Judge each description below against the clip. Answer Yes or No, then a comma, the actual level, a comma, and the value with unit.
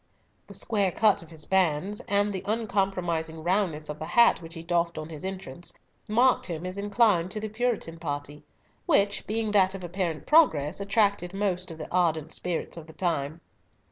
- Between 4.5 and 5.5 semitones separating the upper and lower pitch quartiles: No, average, 3.9 semitones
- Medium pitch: Yes, medium, 180 Hz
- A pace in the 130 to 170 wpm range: No, average, 180 wpm